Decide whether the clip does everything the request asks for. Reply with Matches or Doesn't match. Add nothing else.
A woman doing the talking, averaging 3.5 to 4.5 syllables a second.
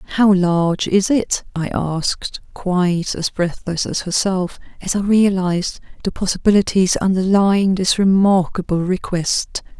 Matches